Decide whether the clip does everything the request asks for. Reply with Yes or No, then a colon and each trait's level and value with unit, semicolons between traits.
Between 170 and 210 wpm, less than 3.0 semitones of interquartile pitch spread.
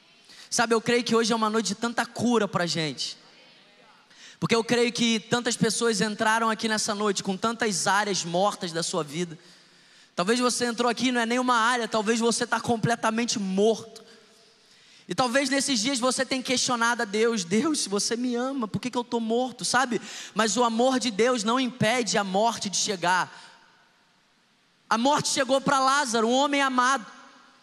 Yes: average, 180 wpm; narrow, 2.4 semitones